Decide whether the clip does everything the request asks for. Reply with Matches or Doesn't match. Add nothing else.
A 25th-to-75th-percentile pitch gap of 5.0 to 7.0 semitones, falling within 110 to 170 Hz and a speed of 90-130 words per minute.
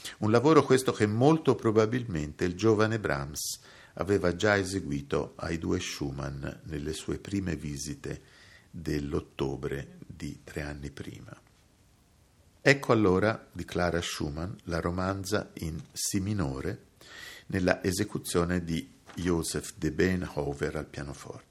Doesn't match